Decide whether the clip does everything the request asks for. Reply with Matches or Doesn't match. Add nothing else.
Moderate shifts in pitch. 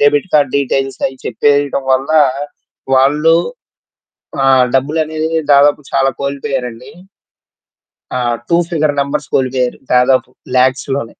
Doesn't match